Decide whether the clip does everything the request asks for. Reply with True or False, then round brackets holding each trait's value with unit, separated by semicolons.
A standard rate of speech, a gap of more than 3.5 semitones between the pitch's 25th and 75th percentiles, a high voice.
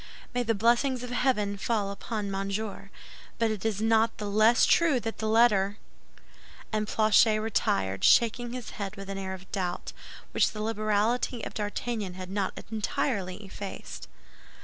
False (155 wpm; 2.6 semitones; 215 Hz)